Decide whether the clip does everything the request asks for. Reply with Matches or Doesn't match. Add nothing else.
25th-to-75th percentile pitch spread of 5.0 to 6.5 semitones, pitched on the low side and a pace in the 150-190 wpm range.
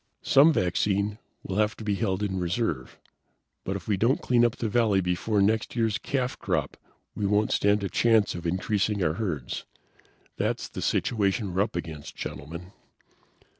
Doesn't match